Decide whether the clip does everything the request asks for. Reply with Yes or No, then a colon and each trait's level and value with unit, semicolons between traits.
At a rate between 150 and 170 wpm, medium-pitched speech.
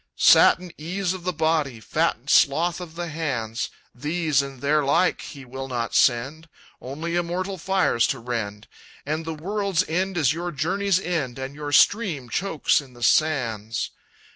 Yes: average, 160 wpm; medium, 155 Hz